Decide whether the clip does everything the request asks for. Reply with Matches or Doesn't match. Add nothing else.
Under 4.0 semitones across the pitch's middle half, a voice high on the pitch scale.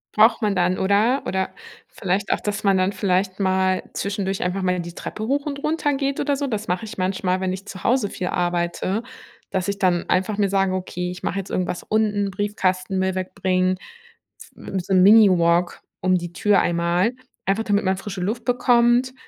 Matches